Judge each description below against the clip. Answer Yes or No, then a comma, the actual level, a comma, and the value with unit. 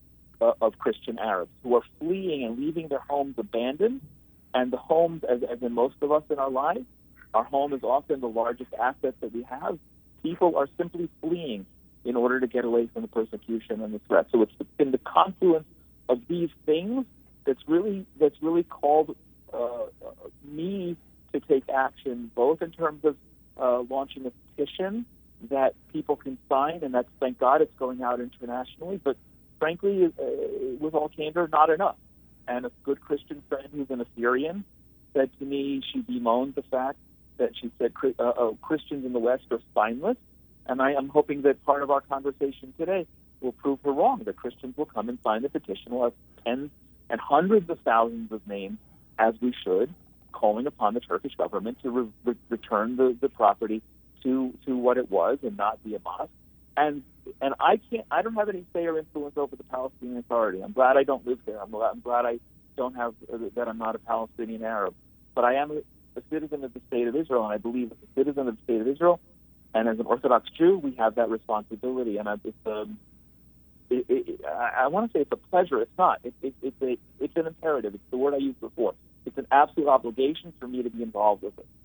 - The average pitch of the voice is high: No, low, 135 Hz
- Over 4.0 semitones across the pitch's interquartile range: Yes, average, 4.5 semitones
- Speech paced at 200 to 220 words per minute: Yes, fast, 205 wpm